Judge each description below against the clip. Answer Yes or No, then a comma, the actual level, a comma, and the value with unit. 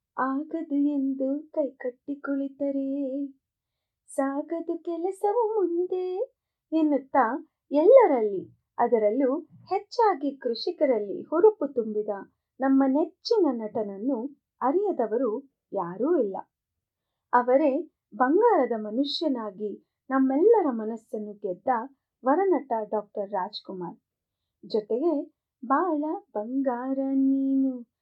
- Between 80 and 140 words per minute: No, average, 70 wpm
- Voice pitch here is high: Yes, very high, 275 Hz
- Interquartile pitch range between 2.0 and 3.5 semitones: No, average, 5.2 semitones